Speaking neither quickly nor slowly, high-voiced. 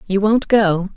Yes: average, 190 wpm; high, 200 Hz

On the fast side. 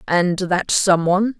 No: slow, 130 wpm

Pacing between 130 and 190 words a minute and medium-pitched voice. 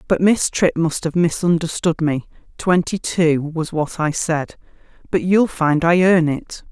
Yes: average, 170 wpm; medium, 165 Hz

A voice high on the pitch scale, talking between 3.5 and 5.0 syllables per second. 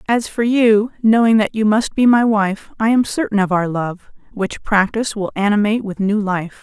Yes: high, 215 Hz; 4.9 syllables/s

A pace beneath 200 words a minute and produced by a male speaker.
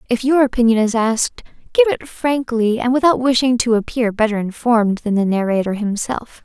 No: average, 175 wpm; female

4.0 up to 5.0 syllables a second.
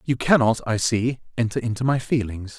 No: 5.2 syllables/s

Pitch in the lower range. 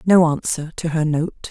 No: medium, 160 Hz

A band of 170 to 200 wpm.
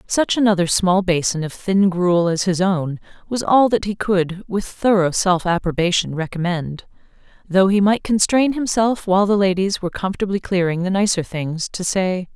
Yes: average, 175 wpm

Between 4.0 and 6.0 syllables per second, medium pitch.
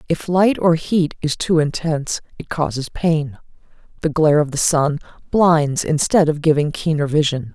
Yes: 4.7 syllables/s; medium, 155 Hz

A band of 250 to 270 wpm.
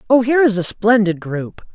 No: fast, 205 wpm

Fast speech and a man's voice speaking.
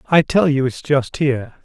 Yes: fast, 220 wpm; male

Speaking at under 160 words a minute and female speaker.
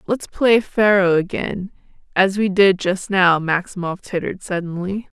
Yes: average, 140 wpm; female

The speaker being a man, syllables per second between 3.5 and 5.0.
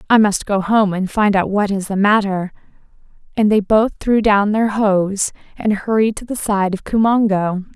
No: female; 4.5 syllables/s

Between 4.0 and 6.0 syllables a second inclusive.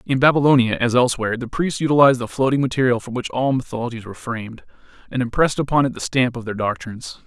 No: 7.1 syllables/s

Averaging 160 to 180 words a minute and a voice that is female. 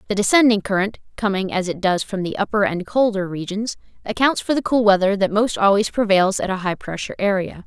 No: average, 195 wpm; female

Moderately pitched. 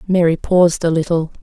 Yes: medium, 170 Hz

